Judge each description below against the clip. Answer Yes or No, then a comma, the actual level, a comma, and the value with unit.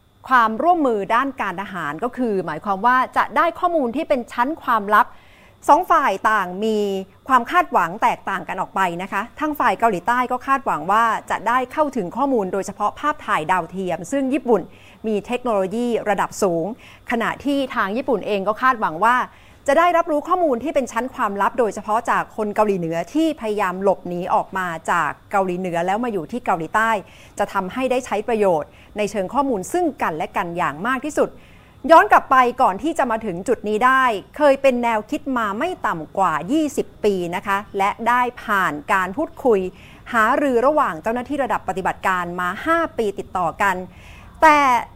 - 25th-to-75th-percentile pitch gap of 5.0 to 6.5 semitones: Yes, wide, 5.6 semitones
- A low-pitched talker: No, high, 225 Hz